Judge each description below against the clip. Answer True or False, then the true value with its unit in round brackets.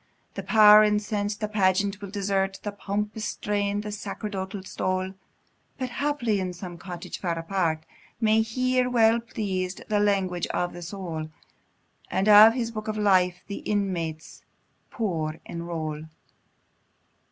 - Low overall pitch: False (200 Hz)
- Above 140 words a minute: False (135 wpm)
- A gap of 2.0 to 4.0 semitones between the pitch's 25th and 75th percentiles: True (2.7 semitones)